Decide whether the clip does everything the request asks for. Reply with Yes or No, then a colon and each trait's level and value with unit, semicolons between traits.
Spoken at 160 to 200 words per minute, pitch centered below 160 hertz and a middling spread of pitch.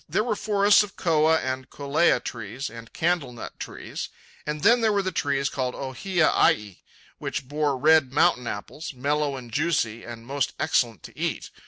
Yes: average, 170 wpm; medium, 140 Hz; average, 5.0 semitones